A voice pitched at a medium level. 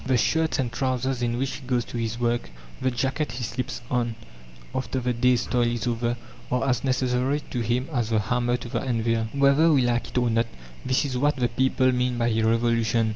No: low, 125 Hz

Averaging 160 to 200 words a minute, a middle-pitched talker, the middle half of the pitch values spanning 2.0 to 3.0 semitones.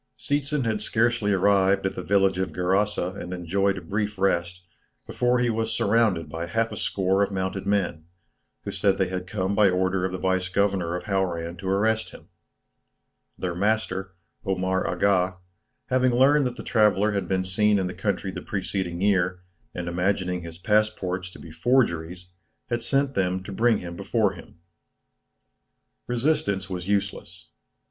No: average, 165 wpm; very low, 95 Hz; average, 2.7 semitones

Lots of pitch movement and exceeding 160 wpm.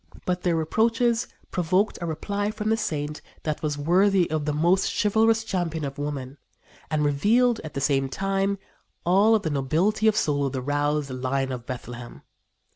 Yes: wide, 5.9 semitones; average, 170 wpm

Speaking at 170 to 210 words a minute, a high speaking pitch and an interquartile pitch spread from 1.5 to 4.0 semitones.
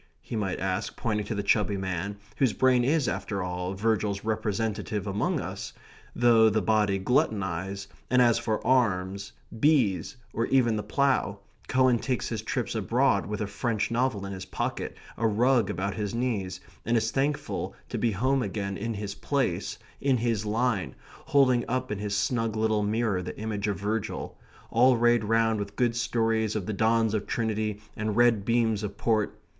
No: average, 175 wpm; low, 110 Hz; average, 2.8 semitones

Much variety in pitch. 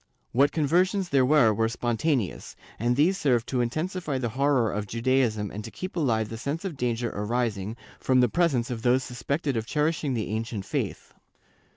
No: average, 4.4 semitones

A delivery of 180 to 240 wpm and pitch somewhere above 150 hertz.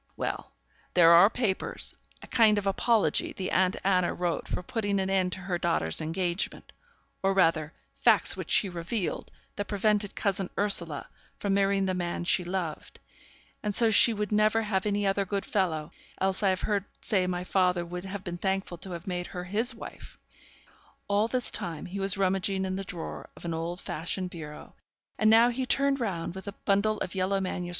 Yes: average, 190 wpm; high, 190 Hz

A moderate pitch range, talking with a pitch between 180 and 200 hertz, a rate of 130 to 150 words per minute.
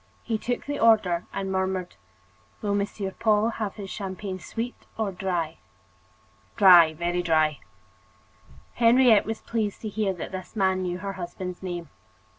Yes: average, 3.3 semitones; high, 190 Hz; average, 145 wpm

